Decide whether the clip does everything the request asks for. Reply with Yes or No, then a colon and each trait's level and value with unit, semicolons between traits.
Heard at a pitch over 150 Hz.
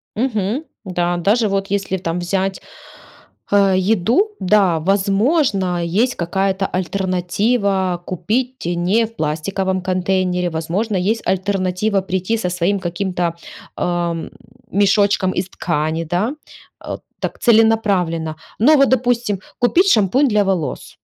Yes: high, 190 Hz